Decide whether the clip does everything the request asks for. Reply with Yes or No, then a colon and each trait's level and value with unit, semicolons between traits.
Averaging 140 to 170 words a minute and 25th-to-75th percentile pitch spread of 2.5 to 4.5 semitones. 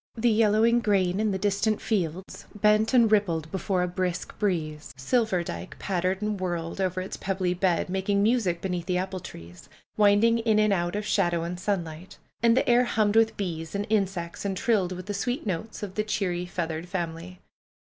No: average, 185 wpm; average, 3.3 semitones